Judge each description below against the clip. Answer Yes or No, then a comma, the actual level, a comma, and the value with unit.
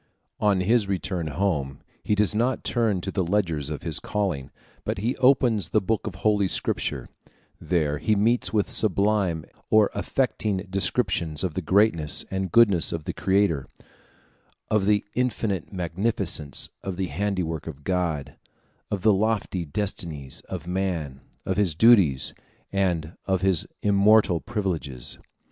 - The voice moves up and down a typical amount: Yes, average, 4.2 semitones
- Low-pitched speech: Yes, very low, 95 Hz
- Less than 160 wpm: Yes, average, 145 wpm